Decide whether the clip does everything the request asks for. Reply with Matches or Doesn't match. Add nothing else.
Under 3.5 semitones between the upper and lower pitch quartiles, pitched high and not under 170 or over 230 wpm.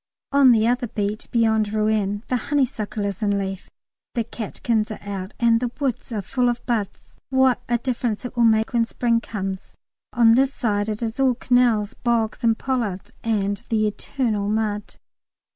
Matches